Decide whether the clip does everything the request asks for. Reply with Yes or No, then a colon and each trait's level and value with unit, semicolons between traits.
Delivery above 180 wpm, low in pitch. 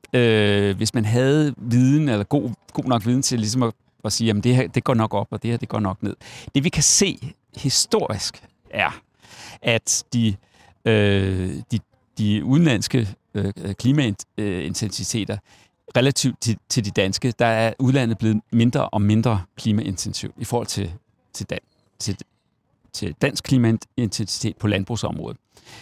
No: average, 155 wpm; low, 115 Hz